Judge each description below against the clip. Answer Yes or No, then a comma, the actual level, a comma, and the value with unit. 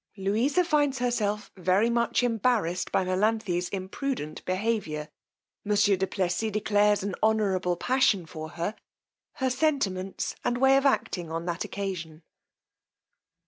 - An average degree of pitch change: Yes, average, 4.6 semitones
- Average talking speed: No, slow, 125 wpm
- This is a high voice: Yes, high, 205 Hz